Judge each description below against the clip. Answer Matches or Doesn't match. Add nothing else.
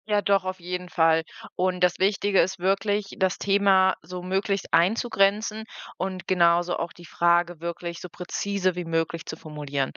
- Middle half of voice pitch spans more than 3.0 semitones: Doesn't match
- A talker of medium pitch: Matches